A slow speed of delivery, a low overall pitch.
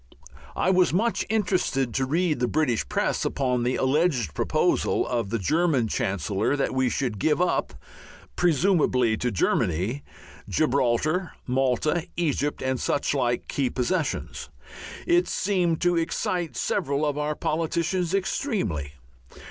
No: slow, 125 wpm; medium, 145 Hz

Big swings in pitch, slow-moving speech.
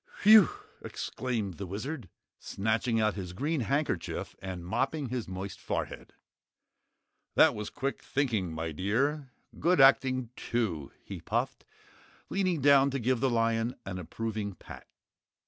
Yes: wide, 5.9 semitones; slow, 130 wpm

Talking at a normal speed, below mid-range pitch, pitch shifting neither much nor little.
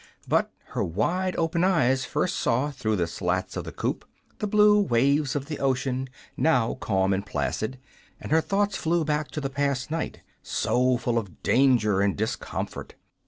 No: average, 170 wpm; low, 130 Hz; wide, 6.1 semitones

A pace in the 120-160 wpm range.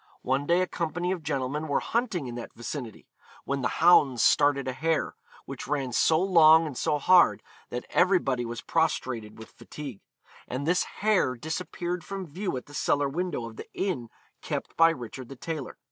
No: average, 180 wpm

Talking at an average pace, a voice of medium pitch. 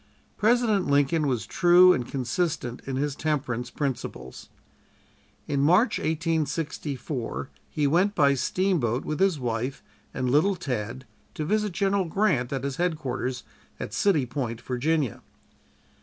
No: slow, 125 wpm; medium, 145 Hz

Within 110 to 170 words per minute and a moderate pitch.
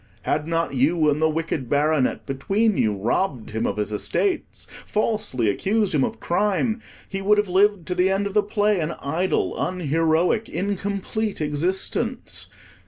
Yes: average, 160 wpm; medium, 180 Hz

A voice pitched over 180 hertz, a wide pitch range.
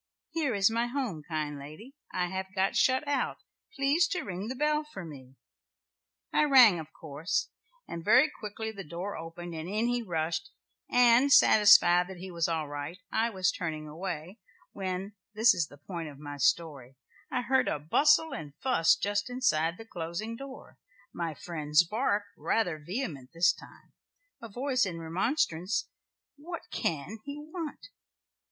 Yes: high, 190 Hz; wide, 7.1 semitones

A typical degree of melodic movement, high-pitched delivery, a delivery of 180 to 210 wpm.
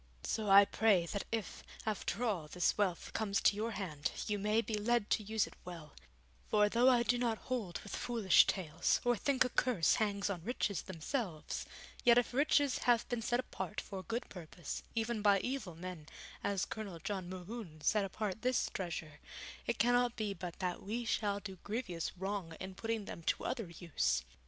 Yes: average, 4.3 semitones; high, 205 Hz; average, 190 wpm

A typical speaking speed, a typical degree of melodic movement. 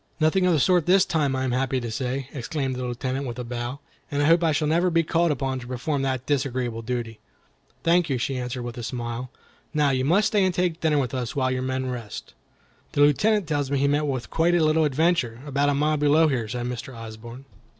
No: fast, 235 wpm; average, 3.9 semitones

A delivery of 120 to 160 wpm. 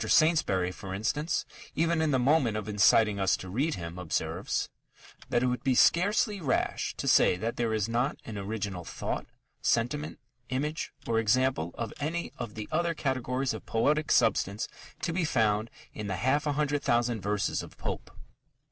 No: average, 175 wpm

